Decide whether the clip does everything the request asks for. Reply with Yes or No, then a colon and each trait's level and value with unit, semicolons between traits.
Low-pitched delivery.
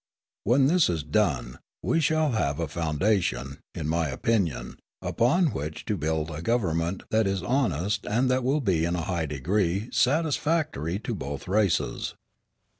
Yes: very low, 95 Hz